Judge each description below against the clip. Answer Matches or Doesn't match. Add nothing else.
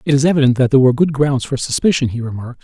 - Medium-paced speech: Doesn't match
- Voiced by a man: Matches